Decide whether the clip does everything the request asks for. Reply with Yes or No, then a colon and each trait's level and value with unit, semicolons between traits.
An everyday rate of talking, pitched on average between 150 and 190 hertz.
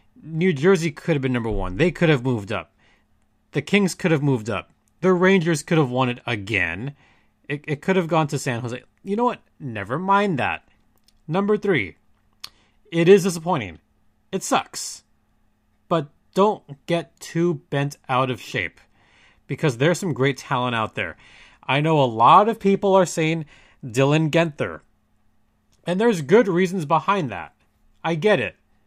No: average, 165 wpm; medium, 140 Hz